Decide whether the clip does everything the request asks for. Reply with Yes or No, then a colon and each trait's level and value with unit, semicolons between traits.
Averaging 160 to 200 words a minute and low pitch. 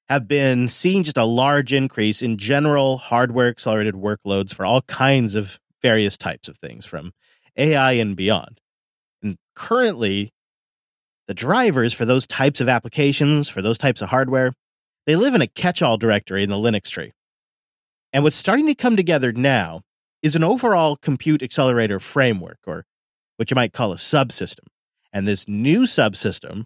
Yes: average, 165 wpm; low, 125 Hz